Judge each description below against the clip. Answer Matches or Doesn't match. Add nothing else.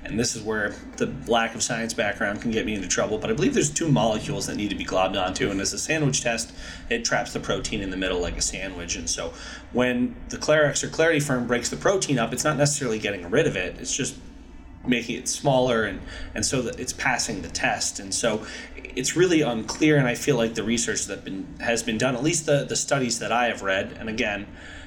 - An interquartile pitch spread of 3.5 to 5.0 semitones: Matches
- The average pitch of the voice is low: Matches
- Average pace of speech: Doesn't match